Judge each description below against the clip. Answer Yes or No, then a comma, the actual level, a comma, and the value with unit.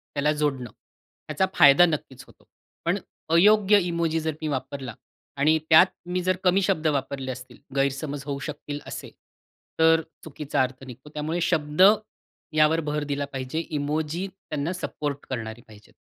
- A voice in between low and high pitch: Yes, medium, 150 Hz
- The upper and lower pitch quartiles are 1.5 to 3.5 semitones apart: Yes, average, 2.9 semitones